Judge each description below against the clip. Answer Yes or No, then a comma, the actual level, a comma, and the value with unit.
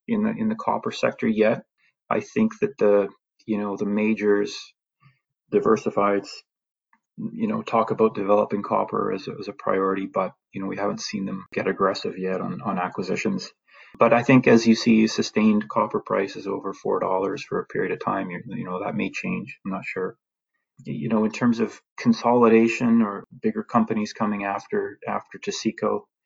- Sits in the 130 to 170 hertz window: No, low, 115 Hz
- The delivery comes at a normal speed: Yes, average, 180 wpm